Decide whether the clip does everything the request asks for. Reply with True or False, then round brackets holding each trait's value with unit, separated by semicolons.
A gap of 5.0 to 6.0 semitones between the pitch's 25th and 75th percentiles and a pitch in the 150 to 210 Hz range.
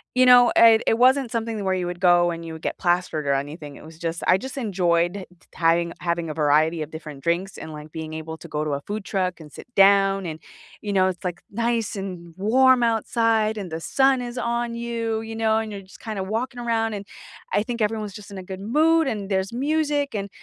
True (5.3 semitones; 195 Hz)